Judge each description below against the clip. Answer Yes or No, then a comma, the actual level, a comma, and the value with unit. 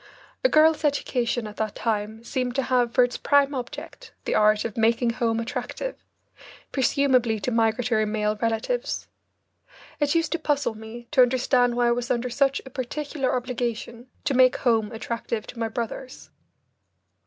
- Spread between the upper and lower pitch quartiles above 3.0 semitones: No, average, 2.7 semitones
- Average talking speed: Yes, average, 160 wpm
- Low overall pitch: No, high, 245 Hz